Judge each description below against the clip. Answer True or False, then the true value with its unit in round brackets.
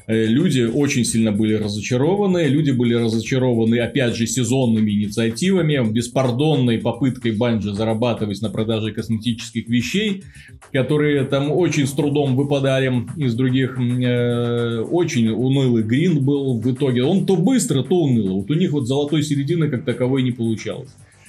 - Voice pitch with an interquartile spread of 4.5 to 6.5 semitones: False (3.7 semitones)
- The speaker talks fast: False (140 wpm)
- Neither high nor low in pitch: False (125 Hz)